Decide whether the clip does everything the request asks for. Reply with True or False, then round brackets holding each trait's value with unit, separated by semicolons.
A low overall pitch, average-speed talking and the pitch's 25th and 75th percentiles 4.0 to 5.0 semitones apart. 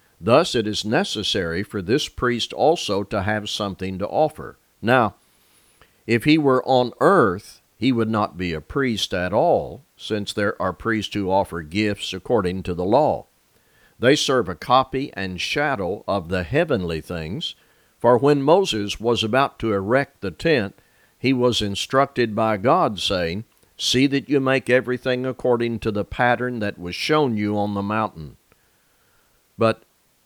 True (110 Hz; 160 wpm; 4.3 semitones)